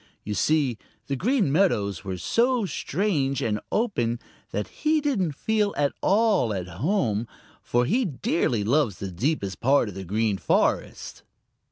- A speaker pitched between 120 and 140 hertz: Yes, low, 135 Hz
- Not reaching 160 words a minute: Yes, average, 150 wpm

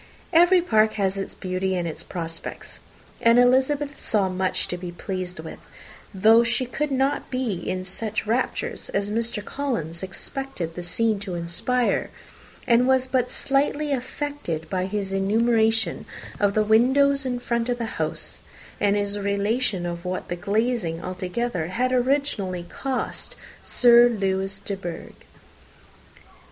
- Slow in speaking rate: No, average, 145 wpm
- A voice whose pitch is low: No, high, 215 Hz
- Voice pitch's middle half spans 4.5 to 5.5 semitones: Yes, average, 5.1 semitones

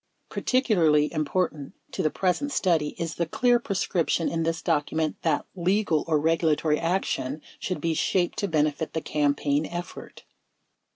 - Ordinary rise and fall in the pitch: Yes, average, 3.1 semitones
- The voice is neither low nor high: Yes, medium, 165 Hz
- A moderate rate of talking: Yes, average, 150 wpm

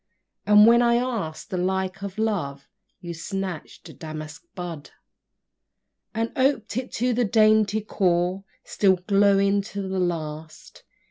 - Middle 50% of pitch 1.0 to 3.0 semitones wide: No, average, 3.8 semitones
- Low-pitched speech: No, high, 195 Hz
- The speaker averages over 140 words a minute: No, slow, 135 wpm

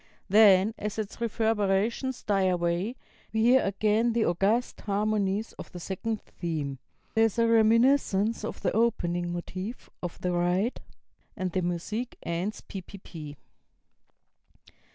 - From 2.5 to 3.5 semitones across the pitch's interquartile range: No, average, 3.9 semitones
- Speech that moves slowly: Yes, slow, 130 wpm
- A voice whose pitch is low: No, high, 205 Hz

